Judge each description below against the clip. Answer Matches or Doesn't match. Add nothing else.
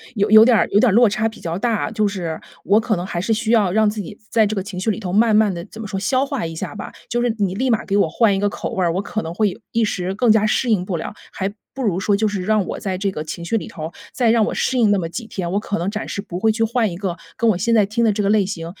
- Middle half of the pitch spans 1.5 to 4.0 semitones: Matches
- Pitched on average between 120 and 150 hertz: Doesn't match